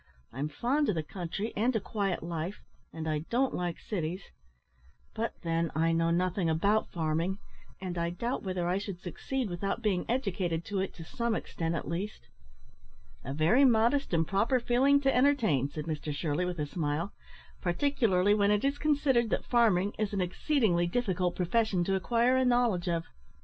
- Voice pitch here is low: No, high, 190 Hz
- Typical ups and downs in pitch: No, wide, 5.7 semitones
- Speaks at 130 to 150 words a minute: No, average, 175 wpm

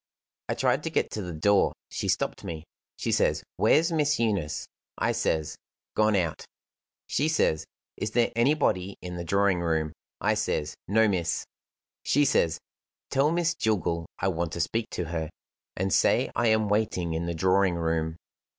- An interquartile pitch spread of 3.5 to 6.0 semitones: Yes, average, 5.0 semitones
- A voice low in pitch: Yes, very low, 95 Hz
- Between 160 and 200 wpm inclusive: Yes, average, 170 wpm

